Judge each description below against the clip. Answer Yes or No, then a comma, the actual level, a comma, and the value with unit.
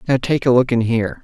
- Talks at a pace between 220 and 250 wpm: No, fast, 295 wpm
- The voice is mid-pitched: No, low, 120 Hz